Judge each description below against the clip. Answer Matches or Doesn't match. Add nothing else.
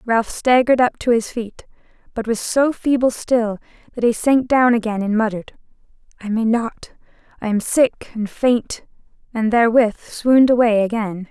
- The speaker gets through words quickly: Doesn't match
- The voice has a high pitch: Matches